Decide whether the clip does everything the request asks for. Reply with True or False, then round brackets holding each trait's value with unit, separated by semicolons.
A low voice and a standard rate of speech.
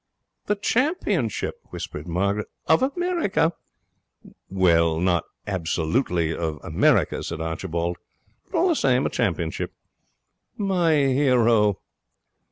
False (105 Hz; 100 wpm)